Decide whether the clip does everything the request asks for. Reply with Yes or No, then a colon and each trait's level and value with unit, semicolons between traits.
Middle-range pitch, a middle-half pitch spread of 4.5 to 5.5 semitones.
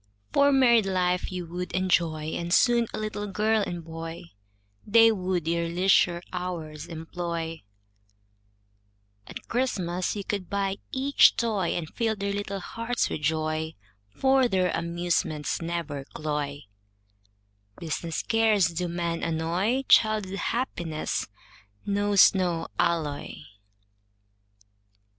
No: medium, 180 Hz; average, 3.9 semitones